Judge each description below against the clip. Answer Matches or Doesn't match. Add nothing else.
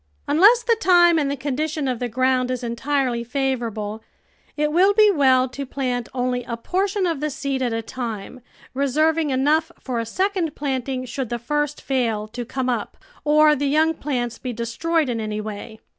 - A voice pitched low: Doesn't match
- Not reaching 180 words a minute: Doesn't match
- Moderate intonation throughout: Matches